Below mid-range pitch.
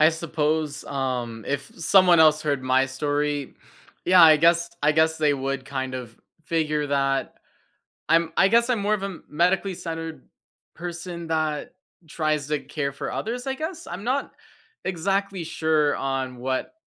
No: medium, 155 Hz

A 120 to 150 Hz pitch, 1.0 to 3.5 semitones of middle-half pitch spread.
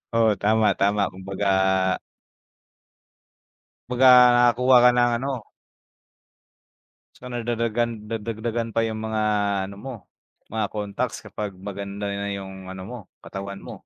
No: low, 110 Hz; average, 2.9 semitones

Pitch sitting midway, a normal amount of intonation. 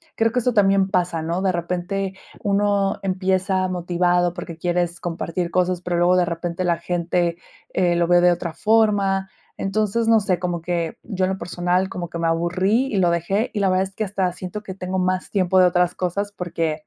No: medium, 180 Hz; narrow, 2.0 semitones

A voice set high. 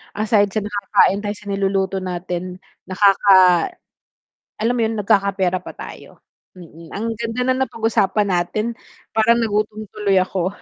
Yes: high, 205 Hz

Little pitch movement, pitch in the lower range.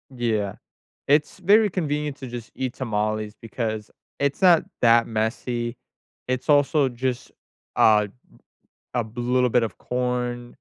No: average, 3.1 semitones; low, 125 Hz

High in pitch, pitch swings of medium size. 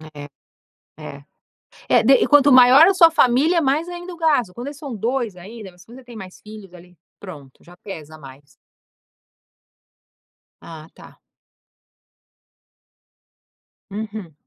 No: high, 220 Hz; wide, 7.9 semitones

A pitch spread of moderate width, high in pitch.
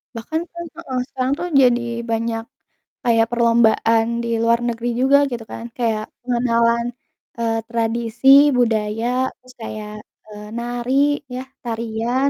No: narrow, 1.4 semitones; high, 235 Hz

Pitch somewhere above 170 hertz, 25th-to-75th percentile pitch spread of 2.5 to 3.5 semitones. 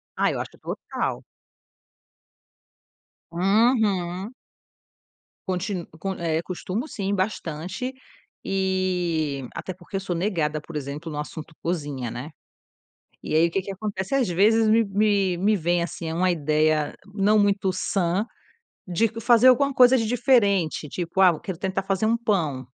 No: medium, 185 Hz; average, 4.0 semitones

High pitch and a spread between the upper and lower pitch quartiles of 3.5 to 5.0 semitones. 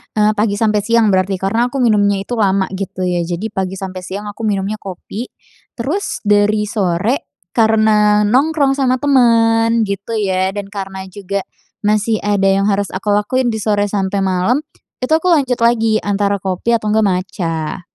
No: high, 205 Hz; average, 2.9 semitones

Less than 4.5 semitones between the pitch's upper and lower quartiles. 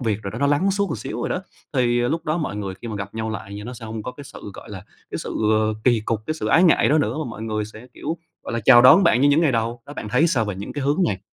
No: average, 5.2 semitones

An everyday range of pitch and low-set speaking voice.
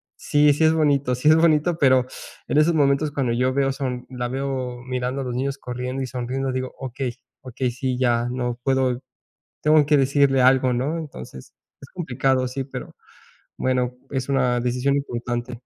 No: narrow, 1.9 semitones; low, 130 Hz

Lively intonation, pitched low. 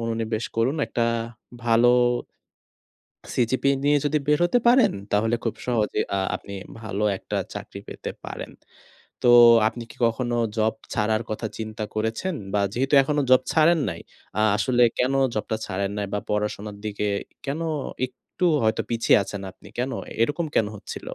No: average, 3.8 semitones; low, 115 Hz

